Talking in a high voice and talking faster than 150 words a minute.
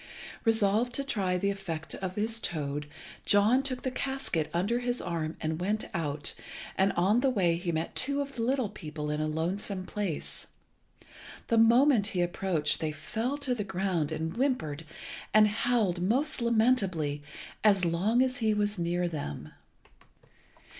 Yes: high, 195 Hz; average, 160 wpm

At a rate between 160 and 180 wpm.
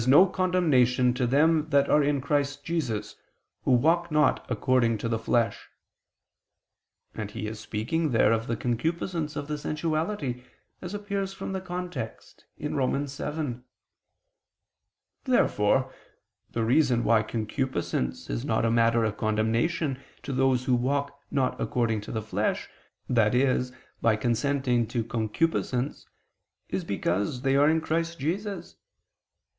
No: slow, 135 wpm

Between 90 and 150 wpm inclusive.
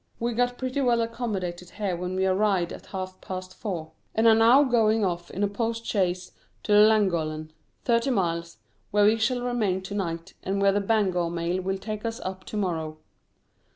No: average, 185 wpm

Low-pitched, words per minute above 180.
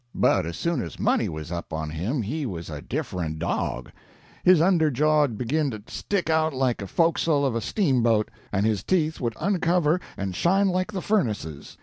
Yes: low, 130 Hz; average, 190 wpm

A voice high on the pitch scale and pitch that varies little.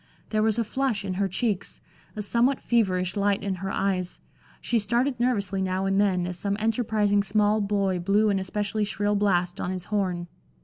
Yes: high, 200 Hz; narrow, 2.1 semitones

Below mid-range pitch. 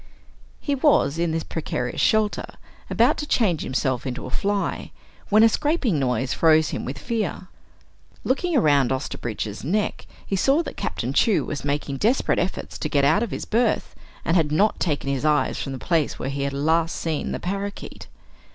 No: medium, 165 Hz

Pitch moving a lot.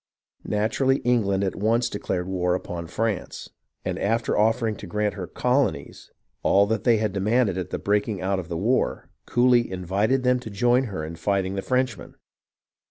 No: average, 3.9 semitones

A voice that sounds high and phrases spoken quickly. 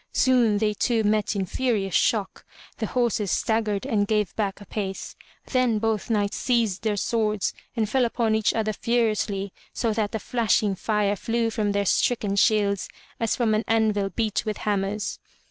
No: high, 215 Hz; average, 170 wpm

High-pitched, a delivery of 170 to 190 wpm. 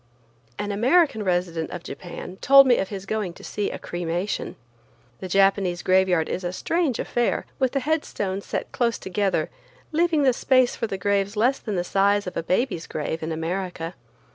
Yes: high, 195 Hz; average, 175 wpm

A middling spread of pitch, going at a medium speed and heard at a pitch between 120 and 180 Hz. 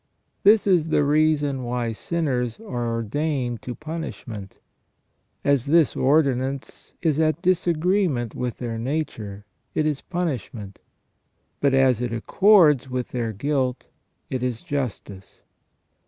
No: average, 4.5 semitones; slow, 125 wpm; low, 135 Hz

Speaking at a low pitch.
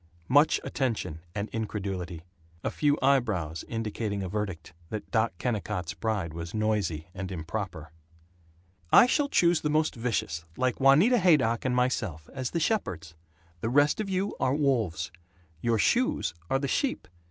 Yes: low, 110 Hz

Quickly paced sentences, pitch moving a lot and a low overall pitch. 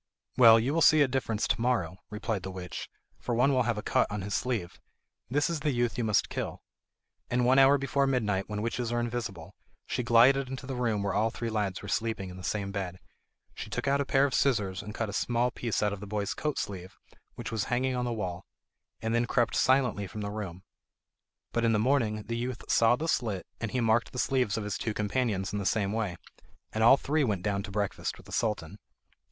No: fast, 235 wpm; average, 3.5 semitones; low, 115 Hz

